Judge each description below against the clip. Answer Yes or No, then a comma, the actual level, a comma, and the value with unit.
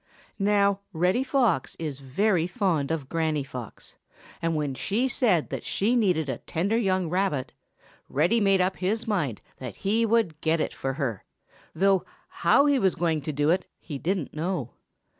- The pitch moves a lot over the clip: No, average, 5.0 semitones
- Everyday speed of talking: Yes, average, 170 wpm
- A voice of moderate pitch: Yes, medium, 175 Hz